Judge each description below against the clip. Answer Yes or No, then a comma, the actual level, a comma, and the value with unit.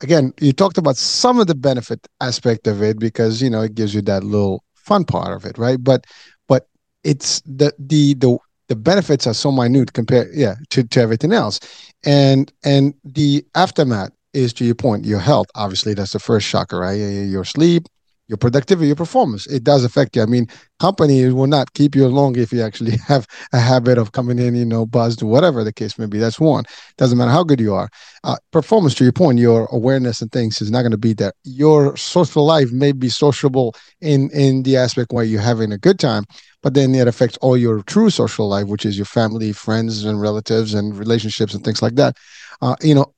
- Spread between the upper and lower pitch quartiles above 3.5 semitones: Yes, average, 4.3 semitones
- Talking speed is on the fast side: Yes, fast, 215 wpm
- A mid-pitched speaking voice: No, low, 125 Hz